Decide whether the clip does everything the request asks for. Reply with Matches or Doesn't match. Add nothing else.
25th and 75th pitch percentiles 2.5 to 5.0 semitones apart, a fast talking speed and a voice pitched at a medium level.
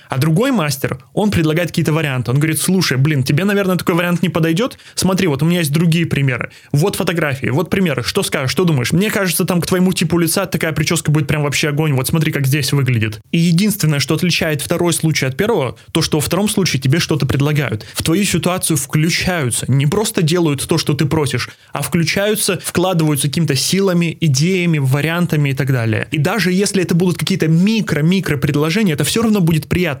Matches